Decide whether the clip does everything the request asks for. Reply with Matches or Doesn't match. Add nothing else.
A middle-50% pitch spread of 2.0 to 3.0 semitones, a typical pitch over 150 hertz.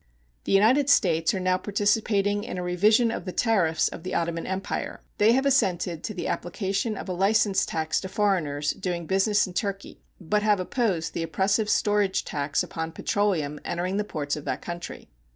Doesn't match